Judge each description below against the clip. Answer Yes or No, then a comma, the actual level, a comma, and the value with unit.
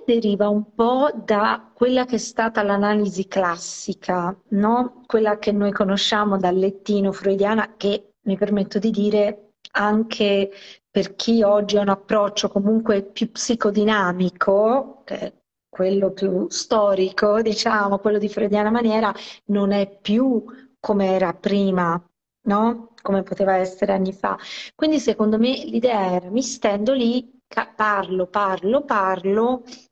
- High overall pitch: Yes, high, 210 Hz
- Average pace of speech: Yes, average, 130 wpm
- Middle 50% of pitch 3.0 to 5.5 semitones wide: No, narrow, 2.4 semitones